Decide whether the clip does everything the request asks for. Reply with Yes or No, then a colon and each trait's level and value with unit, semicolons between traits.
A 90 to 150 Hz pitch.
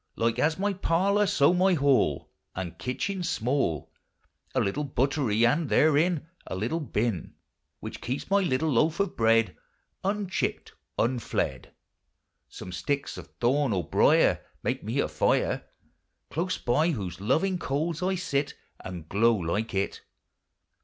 Yes: medium, 140 Hz